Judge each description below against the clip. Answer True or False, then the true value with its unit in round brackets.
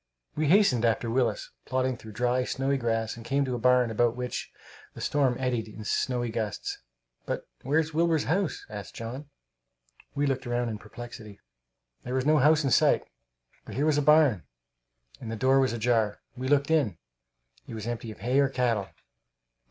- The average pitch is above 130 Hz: False (125 Hz)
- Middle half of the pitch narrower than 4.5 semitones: True (3.5 semitones)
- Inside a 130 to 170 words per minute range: False (180 wpm)